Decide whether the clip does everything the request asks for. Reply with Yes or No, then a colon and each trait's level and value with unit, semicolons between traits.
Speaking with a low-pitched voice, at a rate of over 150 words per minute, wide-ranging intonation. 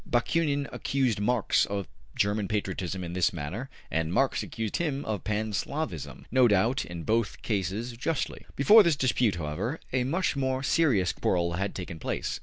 Yes: low, 110 Hz; average, 165 wpm; wide, 6.2 semitones